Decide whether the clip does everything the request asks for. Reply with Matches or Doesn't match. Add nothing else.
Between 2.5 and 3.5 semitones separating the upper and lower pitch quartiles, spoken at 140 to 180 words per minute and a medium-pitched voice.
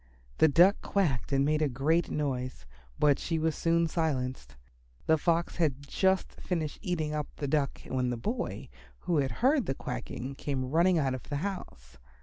Doesn't match